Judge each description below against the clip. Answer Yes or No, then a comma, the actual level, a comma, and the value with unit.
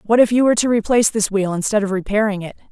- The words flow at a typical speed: No, fast, 265 wpm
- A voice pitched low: No, high, 210 Hz